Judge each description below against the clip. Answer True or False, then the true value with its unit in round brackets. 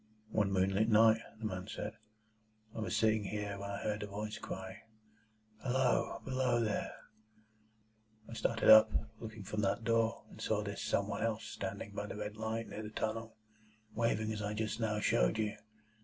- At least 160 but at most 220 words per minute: True (175 wpm)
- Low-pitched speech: True (110 Hz)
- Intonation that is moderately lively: False (1.5 semitones)